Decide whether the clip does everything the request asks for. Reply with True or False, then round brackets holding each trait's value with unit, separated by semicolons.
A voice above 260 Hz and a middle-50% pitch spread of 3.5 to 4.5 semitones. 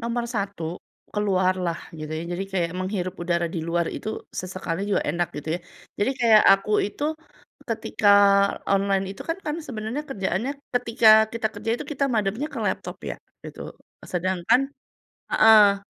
False (200 Hz; 3.9 semitones)